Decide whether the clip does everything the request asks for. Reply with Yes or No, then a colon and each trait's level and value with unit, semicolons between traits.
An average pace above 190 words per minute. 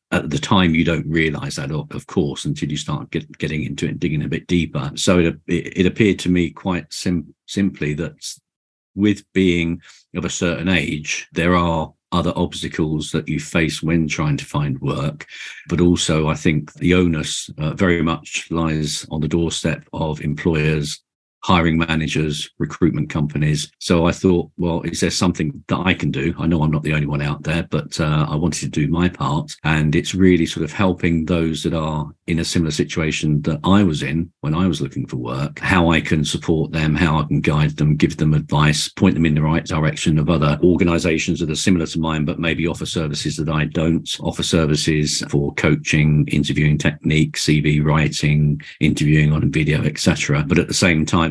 Yes: average, 200 wpm